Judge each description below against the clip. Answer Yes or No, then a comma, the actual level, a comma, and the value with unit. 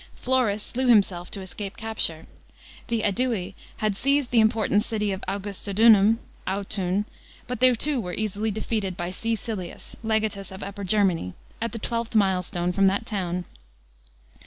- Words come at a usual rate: Yes, average, 150 wpm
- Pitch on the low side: No, high, 205 Hz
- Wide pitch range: No, average, 2.9 semitones